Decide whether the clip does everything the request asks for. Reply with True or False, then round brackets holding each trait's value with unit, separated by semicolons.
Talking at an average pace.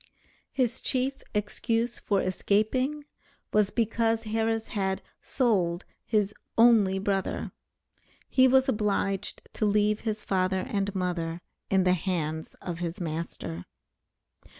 False (115 wpm)